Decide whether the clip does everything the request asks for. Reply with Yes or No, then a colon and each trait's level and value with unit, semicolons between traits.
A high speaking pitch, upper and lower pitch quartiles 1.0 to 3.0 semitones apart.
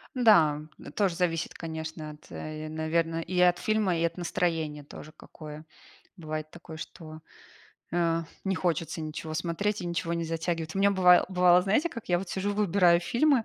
No: medium, 170 Hz; narrow, 2.6 semitones